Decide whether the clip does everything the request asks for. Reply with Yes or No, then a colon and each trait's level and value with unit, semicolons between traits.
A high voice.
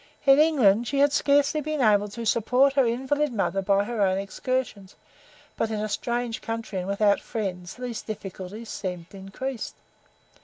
Yes: high, 225 Hz